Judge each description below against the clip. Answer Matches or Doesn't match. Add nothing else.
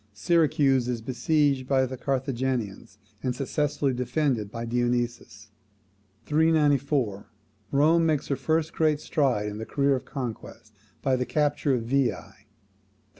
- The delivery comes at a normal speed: Doesn't match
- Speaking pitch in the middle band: Doesn't match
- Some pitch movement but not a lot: Matches